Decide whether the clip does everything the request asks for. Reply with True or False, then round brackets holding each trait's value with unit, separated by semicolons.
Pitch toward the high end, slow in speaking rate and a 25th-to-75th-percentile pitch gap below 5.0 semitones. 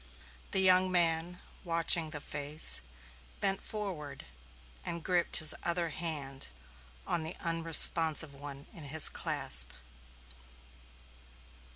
False (165 Hz; 100 wpm; 2.7 semitones)